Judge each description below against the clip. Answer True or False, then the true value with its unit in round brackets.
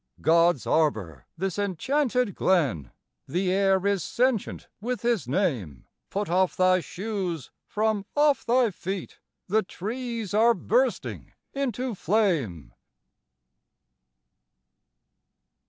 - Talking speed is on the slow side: True (100 wpm)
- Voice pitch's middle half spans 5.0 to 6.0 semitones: True (5.4 semitones)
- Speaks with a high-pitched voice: True (195 Hz)